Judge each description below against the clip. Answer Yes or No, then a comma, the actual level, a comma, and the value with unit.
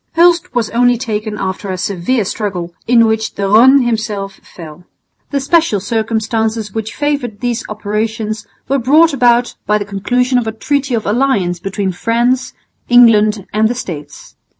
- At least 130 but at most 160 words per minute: Yes, average, 155 wpm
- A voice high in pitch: Yes, high, 220 Hz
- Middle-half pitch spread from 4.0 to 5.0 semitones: No, average, 3.2 semitones